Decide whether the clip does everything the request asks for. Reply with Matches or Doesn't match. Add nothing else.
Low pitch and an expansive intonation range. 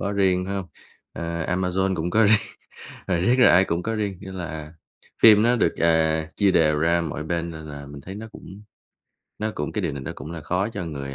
Doesn't match